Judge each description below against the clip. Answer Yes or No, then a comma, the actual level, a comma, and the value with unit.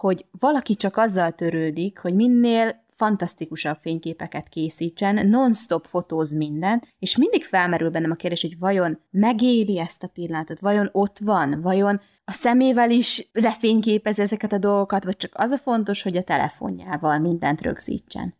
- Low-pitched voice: No, high, 195 Hz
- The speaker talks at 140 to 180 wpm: Yes, average, 150 wpm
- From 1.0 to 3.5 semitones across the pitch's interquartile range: No, average, 4.7 semitones